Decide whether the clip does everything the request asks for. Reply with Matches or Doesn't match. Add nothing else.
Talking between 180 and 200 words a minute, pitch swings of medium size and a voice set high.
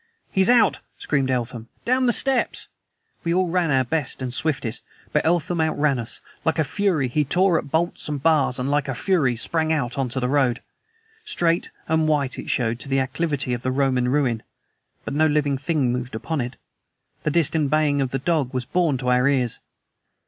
Doesn't match